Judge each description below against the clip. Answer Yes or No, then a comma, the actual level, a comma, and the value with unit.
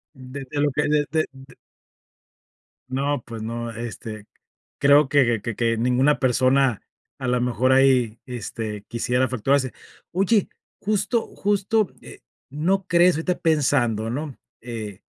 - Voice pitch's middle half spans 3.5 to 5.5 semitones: Yes, average, 4.0 semitones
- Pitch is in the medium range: No, low, 130 Hz